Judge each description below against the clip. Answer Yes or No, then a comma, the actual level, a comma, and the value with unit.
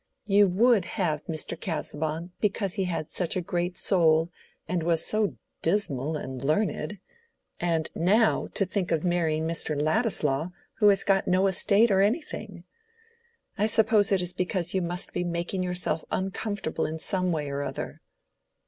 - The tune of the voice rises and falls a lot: No, average, 3.7 semitones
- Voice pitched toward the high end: No, medium, 180 Hz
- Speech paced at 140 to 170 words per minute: Yes, average, 165 wpm